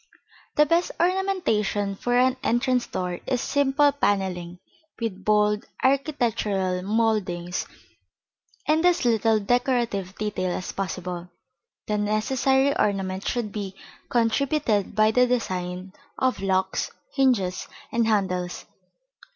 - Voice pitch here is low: No, high, 215 Hz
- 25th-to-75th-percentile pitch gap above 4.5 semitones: Yes, average, 5.0 semitones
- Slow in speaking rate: Yes, slow, 110 wpm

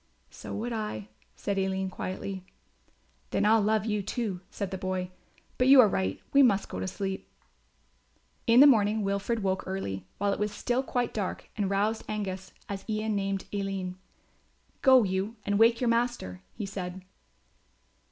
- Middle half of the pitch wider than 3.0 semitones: No, average, 2.7 semitones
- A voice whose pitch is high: Yes, high, 200 Hz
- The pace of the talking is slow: No, average, 165 wpm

